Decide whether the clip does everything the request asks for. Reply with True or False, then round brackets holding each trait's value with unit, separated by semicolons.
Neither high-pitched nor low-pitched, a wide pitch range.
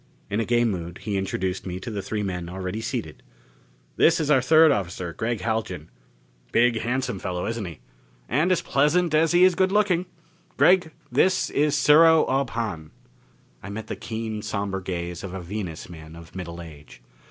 False (110 Hz; 8.1 semitones)